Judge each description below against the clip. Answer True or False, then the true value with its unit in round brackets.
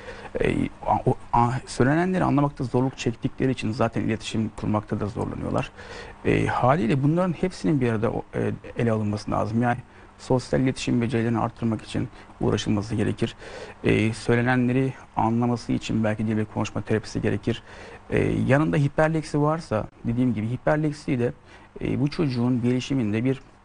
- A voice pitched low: True (120 Hz)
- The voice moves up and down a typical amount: True (3.5 semitones)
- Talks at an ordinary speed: True (125 wpm)